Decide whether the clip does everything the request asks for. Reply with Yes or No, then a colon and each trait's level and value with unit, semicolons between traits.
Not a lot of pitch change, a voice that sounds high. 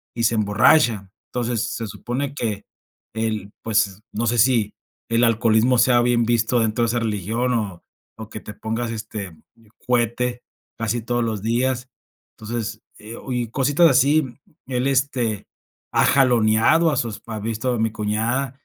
No: narrow, 2.3 semitones; low, 115 Hz